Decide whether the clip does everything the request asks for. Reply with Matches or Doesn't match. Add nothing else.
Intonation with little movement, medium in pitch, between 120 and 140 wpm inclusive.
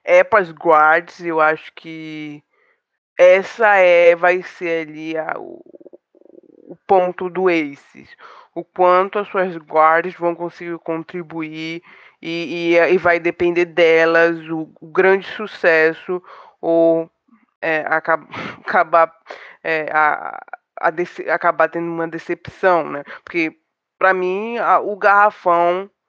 Matches